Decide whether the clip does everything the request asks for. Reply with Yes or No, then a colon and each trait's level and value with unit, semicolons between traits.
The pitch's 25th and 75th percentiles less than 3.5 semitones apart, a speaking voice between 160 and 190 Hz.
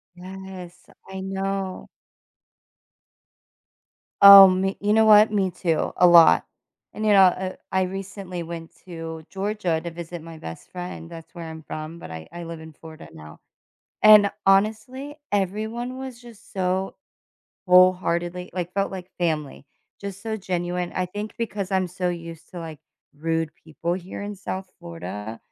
Yes: average, 2.8 semitones; medium, 185 Hz